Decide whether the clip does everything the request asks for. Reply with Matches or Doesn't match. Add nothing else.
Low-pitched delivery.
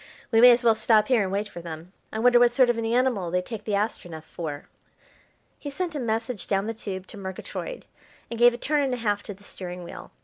Doesn't match